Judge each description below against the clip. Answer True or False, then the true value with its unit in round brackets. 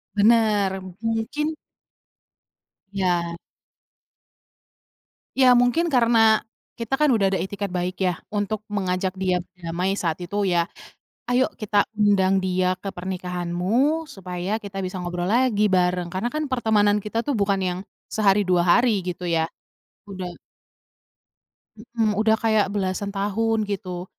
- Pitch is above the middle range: True (200 Hz)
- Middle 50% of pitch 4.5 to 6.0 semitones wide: False (3.4 semitones)